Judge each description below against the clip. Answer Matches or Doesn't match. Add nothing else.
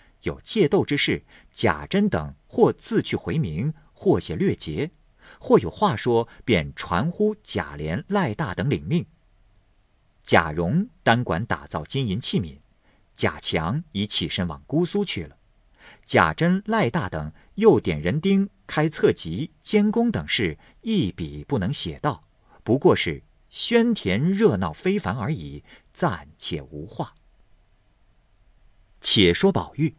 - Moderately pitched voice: Doesn't match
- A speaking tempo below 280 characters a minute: Matches